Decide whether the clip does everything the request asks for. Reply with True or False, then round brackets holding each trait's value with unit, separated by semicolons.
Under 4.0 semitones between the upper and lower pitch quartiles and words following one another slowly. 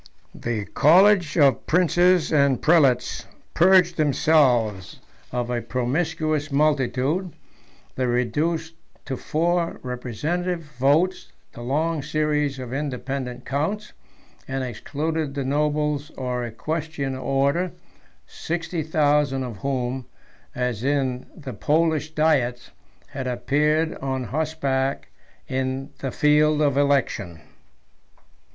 True (3.6 semitones; 105 wpm)